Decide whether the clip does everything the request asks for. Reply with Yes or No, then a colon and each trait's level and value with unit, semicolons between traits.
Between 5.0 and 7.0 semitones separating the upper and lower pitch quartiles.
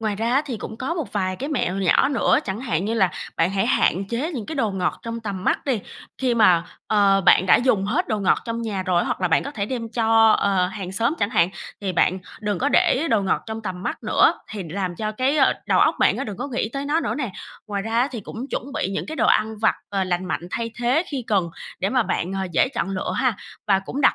No: average, 4.5 semitones